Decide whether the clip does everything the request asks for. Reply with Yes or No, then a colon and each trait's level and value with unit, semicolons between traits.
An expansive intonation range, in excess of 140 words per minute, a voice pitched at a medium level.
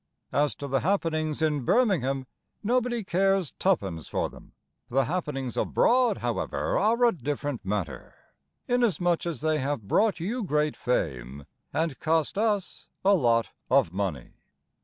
No: wide, 7.3 semitones; slow, 135 wpm; medium, 155 Hz